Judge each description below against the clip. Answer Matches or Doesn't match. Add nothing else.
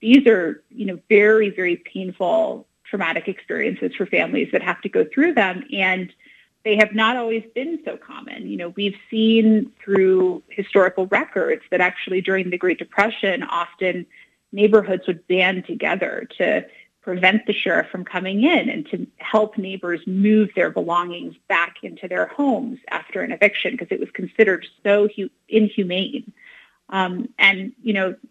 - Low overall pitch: Doesn't match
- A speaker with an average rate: Matches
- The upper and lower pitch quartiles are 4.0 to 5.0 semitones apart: Doesn't match